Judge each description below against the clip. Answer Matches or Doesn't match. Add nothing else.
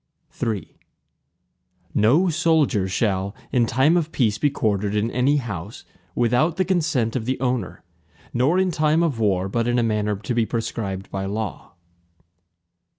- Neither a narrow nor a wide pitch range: Doesn't match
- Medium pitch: Doesn't match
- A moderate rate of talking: Matches